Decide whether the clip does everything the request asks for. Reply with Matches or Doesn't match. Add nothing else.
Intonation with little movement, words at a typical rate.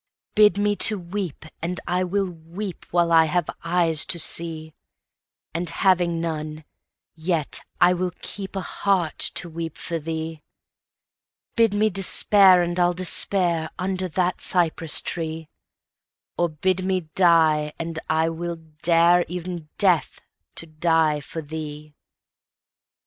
Doesn't match